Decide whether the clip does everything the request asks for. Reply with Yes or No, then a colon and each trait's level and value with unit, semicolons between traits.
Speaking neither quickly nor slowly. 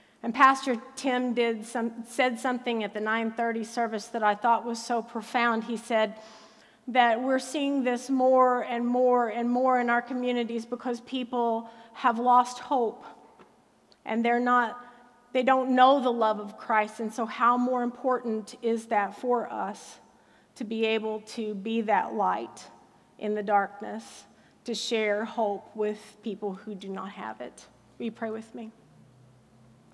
Yes: average, 160 wpm